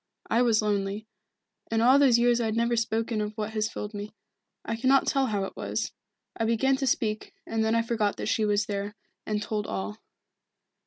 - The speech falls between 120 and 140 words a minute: No, fast, 205 wpm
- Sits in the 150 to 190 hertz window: No, high, 220 Hz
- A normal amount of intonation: No, narrow, 2.0 semitones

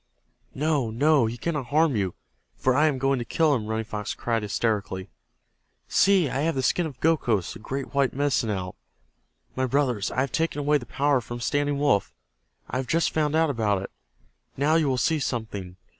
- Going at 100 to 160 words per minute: No, average, 195 wpm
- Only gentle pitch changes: No, average, 4.8 semitones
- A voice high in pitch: No, low, 130 Hz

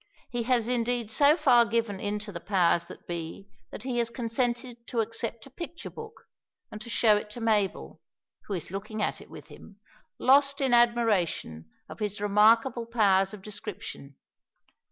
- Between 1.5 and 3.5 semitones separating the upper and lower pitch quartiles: Yes, average, 2.9 semitones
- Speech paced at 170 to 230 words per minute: Yes, average, 175 wpm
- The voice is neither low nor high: No, high, 225 Hz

